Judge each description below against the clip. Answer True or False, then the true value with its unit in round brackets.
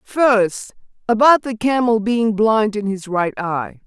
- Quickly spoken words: False (155 wpm)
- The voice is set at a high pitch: True (215 Hz)